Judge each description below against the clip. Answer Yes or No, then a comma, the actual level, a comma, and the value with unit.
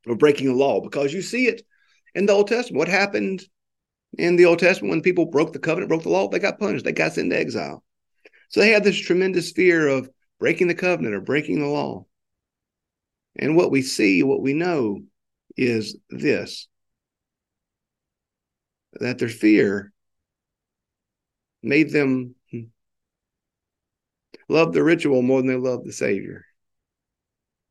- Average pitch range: No, wide, 6.8 semitones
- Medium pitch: Yes, medium, 145 Hz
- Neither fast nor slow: Yes, average, 155 wpm